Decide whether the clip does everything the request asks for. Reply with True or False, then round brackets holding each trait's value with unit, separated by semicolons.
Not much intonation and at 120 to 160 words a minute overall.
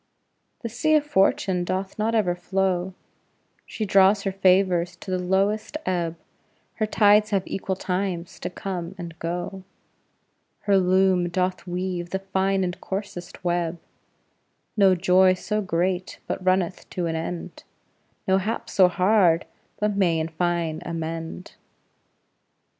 True (1.8 semitones; 135 wpm)